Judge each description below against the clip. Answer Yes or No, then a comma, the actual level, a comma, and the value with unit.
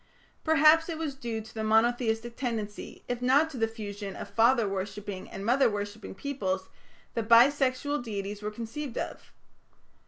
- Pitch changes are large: No, average, 4.1 semitones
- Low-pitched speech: No, high, 230 Hz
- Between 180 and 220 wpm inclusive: No, average, 160 wpm